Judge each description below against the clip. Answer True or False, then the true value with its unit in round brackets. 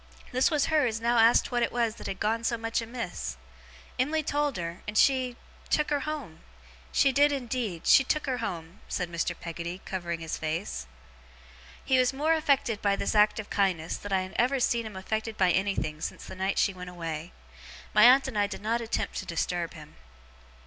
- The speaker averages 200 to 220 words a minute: True (205 wpm)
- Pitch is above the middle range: True (220 Hz)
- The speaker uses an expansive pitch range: True (6.1 semitones)